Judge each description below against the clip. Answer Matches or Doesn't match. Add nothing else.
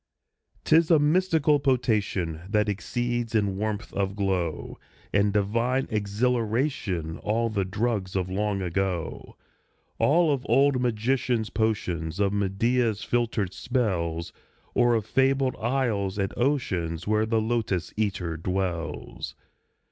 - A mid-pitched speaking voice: Doesn't match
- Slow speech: Matches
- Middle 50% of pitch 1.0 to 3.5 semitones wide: Doesn't match